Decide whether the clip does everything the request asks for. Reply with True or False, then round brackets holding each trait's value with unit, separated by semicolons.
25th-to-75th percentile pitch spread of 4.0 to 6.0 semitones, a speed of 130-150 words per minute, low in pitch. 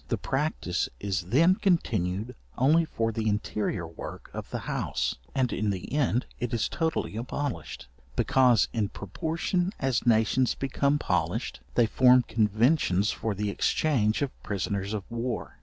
True (4.9 semitones; 145 wpm; 115 Hz)